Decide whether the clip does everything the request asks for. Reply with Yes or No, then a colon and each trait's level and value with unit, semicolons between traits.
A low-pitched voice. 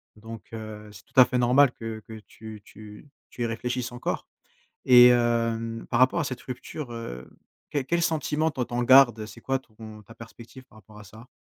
Yes: low, 120 Hz